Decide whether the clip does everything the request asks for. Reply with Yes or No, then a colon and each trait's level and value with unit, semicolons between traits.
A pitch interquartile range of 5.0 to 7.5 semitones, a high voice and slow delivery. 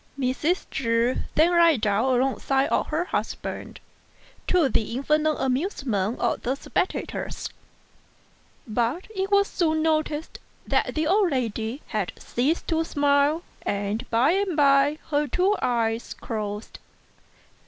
Yes: average, 5.3 semitones; very high, 280 Hz; slow, 125 wpm